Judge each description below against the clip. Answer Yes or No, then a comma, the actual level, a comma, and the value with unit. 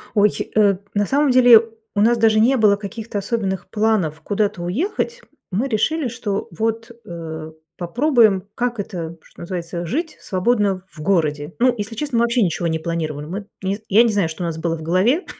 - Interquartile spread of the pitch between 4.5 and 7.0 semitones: Yes, average, 5.3 semitones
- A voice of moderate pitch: No, high, 205 Hz